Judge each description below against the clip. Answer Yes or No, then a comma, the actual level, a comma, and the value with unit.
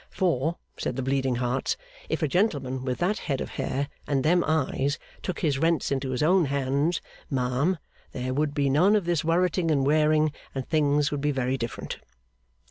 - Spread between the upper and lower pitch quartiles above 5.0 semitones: No, average, 3.6 semitones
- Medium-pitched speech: Yes, medium, 145 Hz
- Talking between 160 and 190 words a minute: Yes, average, 185 wpm